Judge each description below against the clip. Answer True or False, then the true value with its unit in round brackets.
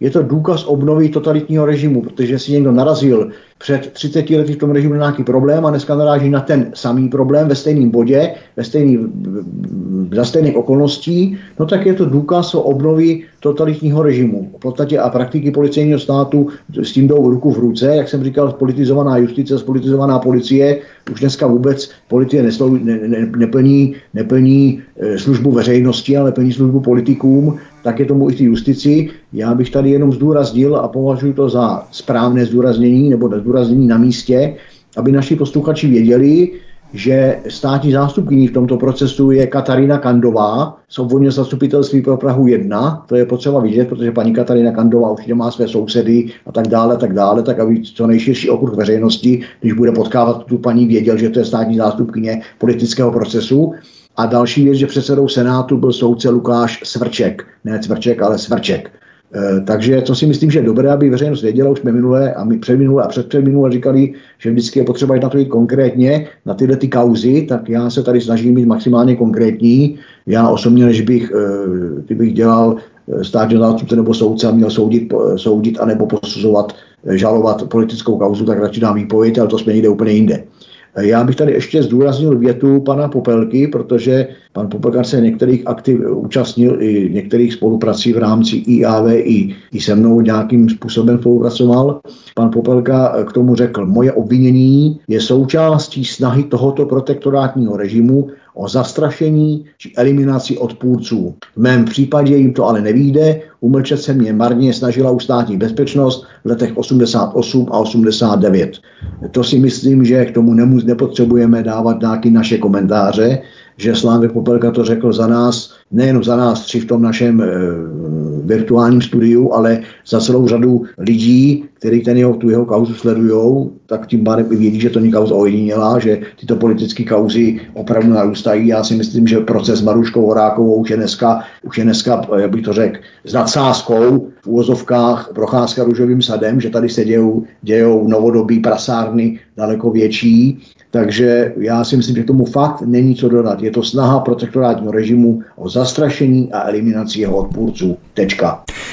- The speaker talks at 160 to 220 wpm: True (165 wpm)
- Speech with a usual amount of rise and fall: True (3.2 semitones)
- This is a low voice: True (120 Hz)